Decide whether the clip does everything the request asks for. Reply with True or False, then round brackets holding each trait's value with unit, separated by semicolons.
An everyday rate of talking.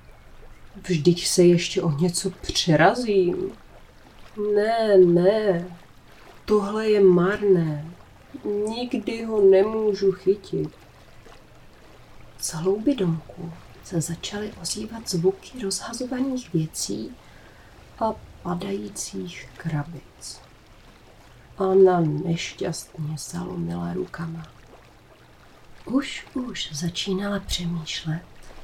False (75 wpm)